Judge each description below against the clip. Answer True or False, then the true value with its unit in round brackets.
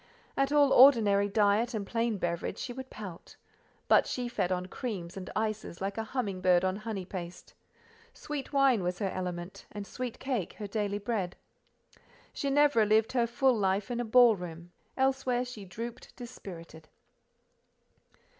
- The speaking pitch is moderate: False (215 Hz)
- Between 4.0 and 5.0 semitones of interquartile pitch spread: True (4.7 semitones)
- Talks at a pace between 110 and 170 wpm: True (155 wpm)